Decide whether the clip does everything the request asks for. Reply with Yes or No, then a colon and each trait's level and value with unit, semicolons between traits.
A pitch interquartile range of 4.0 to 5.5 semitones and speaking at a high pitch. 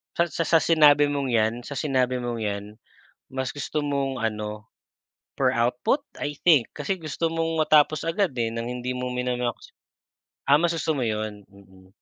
No: average, 4.7 semitones; low, 130 Hz